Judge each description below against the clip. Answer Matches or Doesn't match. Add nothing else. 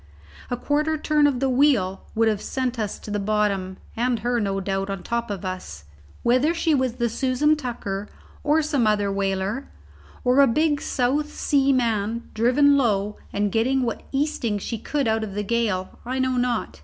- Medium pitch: Doesn't match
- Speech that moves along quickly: Doesn't match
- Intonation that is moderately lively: Matches